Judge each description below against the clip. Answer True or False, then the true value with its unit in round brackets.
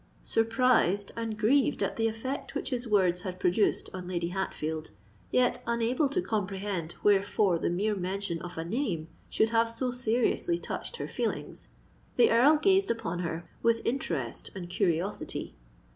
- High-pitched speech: True (210 Hz)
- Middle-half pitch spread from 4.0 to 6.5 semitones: True (4.9 semitones)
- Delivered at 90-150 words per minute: True (145 wpm)